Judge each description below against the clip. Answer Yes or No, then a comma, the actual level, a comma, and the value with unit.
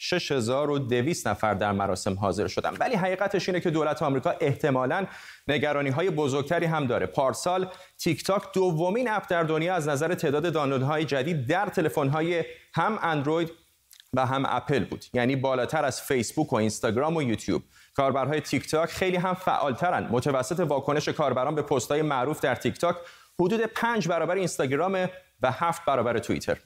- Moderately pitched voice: Yes, medium, 155 Hz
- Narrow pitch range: No, average, 4.8 semitones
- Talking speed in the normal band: No, fast, 160 wpm